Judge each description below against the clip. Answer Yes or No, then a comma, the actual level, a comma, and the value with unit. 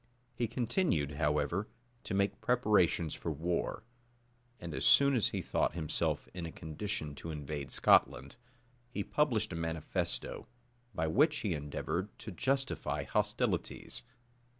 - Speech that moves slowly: Yes, slow, 130 wpm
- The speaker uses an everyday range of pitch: No, wide, 6.8 semitones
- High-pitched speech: No, very low, 90 Hz